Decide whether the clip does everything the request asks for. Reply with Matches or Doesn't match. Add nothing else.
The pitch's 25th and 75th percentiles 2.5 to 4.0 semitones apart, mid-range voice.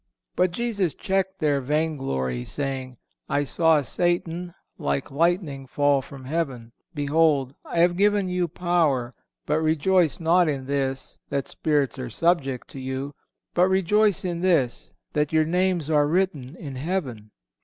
Doesn't match